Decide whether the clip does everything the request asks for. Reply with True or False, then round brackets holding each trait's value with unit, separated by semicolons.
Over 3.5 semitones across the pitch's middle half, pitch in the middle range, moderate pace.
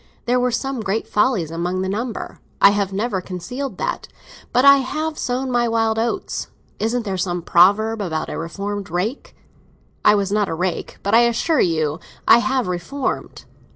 False (5.1 semitones; 215 Hz; 170 wpm)